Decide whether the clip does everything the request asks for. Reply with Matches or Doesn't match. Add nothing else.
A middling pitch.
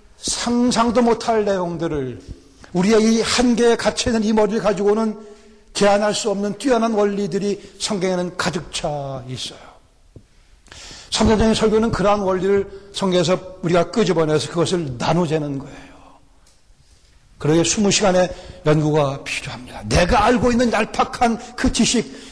Doesn't match